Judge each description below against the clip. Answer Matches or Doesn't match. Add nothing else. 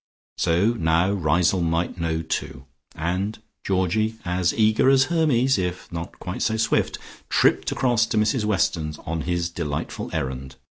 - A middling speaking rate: Matches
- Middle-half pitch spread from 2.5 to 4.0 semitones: Doesn't match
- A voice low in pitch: Matches